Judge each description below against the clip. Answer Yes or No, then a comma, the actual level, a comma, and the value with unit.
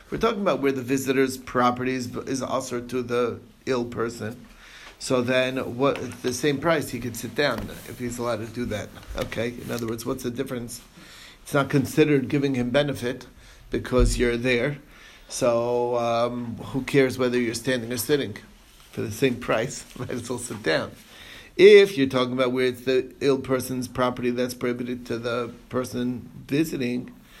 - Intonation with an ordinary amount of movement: No, narrow, 1.6 semitones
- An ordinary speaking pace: Yes, average, 175 wpm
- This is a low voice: Yes, low, 125 Hz